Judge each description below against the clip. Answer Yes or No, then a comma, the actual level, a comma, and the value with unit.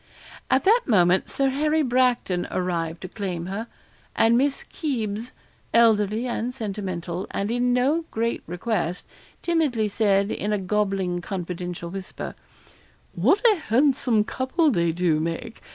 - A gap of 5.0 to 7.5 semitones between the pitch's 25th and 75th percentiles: Yes, wide, 5.6 semitones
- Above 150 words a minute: No, slow, 135 wpm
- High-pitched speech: Yes, high, 210 Hz